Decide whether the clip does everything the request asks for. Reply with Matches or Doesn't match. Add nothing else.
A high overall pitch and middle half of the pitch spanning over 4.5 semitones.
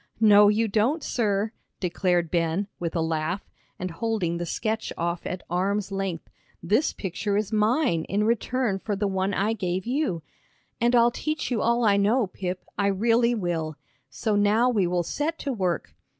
Doesn't match